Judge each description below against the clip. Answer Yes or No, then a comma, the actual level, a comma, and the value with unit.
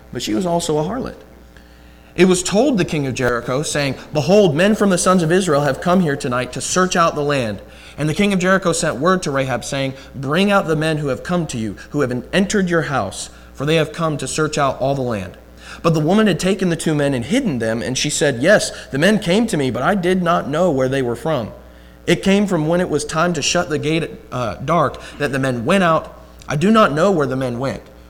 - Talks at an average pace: No, fast, 255 wpm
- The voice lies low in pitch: No, medium, 150 Hz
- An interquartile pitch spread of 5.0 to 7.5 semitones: Yes, wide, 5.5 semitones